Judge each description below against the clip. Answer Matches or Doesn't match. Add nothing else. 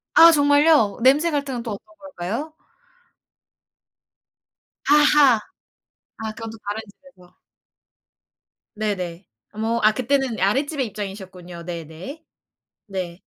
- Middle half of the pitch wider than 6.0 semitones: Matches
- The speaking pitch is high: Matches